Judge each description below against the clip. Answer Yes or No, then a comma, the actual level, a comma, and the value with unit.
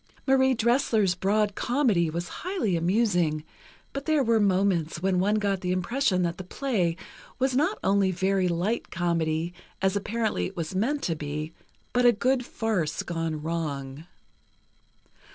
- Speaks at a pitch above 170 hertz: Yes, high, 190 Hz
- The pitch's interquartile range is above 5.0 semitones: Yes, wide, 5.5 semitones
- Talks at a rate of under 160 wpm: Yes, average, 150 wpm